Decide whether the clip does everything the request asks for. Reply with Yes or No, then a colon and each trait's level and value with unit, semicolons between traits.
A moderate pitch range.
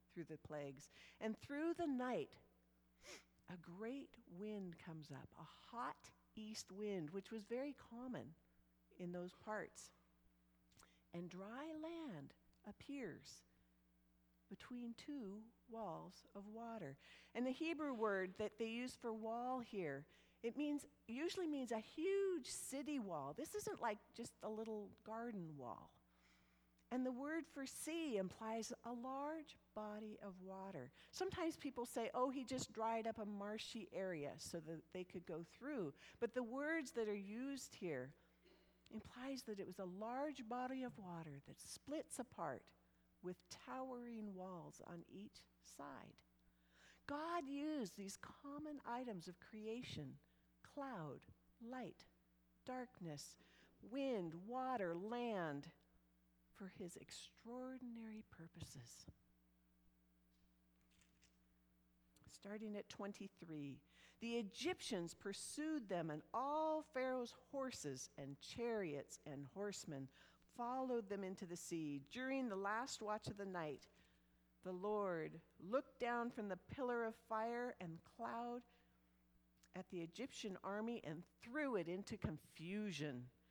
No: wide, 8.7 semitones